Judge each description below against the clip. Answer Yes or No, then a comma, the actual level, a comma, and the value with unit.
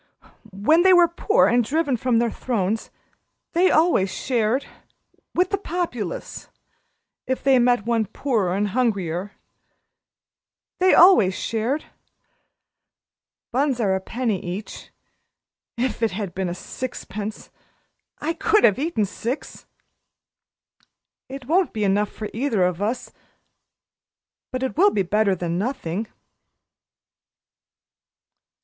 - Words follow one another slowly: Yes, slow, 115 wpm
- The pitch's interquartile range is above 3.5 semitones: Yes, wide, 5.6 semitones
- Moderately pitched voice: No, high, 230 Hz